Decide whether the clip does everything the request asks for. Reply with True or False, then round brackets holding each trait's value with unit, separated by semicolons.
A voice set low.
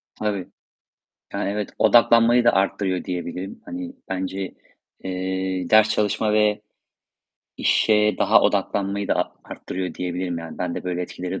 True (95 Hz)